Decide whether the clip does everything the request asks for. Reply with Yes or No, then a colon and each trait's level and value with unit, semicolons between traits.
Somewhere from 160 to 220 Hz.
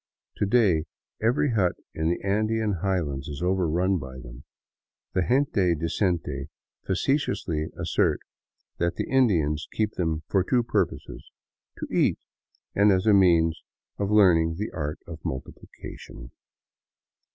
No: very low, 90 Hz